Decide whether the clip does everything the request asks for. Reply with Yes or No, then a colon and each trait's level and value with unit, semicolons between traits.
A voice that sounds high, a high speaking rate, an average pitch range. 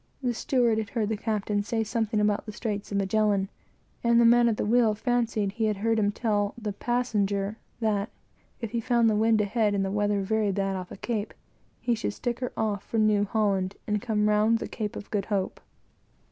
No: high, 215 Hz; fast, 215 wpm; narrow, 2.0 semitones